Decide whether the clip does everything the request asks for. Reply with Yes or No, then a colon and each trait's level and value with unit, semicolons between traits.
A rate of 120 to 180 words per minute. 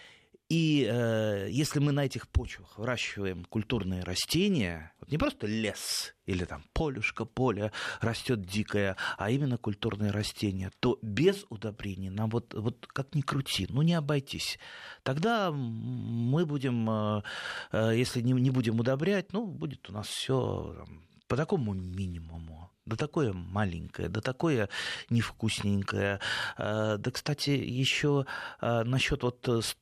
Yes: average, 135 wpm